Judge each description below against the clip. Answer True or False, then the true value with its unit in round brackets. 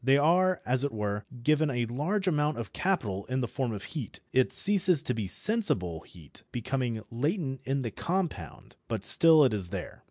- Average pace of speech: True (190 wpm)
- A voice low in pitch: True (130 Hz)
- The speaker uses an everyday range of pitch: False (6.3 semitones)